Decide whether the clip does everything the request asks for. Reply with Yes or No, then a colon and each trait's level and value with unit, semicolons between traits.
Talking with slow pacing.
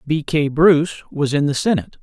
No: fast, 205 wpm